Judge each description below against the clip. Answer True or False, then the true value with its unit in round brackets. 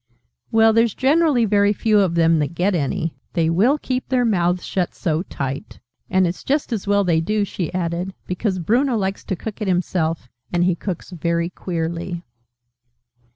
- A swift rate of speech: False (175 wpm)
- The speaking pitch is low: False (185 Hz)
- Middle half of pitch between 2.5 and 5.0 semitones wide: True (4.2 semitones)